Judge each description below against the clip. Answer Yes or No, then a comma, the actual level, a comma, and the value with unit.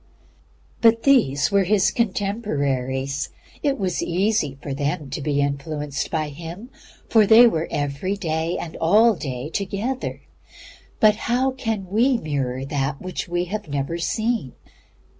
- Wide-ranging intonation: Yes, wide, 7.1 semitones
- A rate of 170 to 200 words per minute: No, average, 140 wpm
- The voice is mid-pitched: Yes, medium, 170 Hz